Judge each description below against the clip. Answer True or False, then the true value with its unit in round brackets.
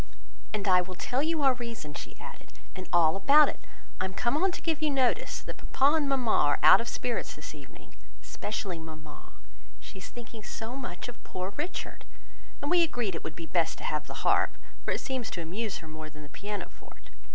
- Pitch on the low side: False (215 Hz)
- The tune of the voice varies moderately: False (7.5 semitones)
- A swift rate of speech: True (220 wpm)